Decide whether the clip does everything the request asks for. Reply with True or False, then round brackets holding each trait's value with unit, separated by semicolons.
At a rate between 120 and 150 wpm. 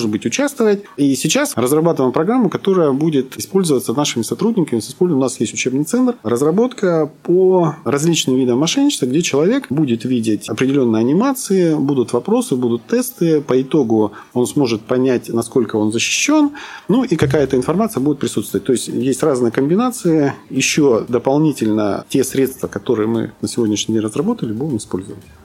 True (145 wpm)